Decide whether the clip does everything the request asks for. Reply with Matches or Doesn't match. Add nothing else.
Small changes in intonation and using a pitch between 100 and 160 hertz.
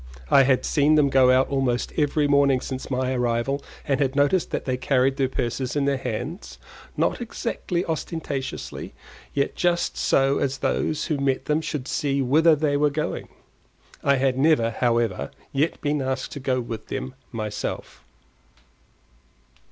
Matches